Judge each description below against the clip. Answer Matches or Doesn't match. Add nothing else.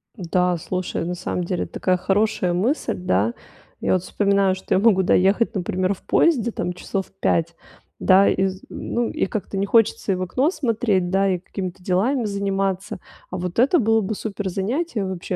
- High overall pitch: Matches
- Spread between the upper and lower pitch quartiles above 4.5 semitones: Doesn't match